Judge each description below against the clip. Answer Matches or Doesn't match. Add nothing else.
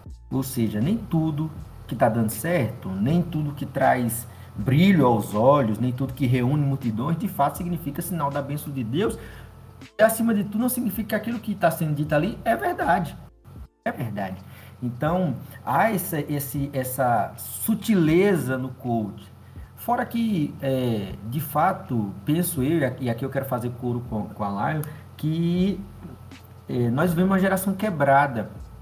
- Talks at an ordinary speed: Matches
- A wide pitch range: Matches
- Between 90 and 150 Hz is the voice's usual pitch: Matches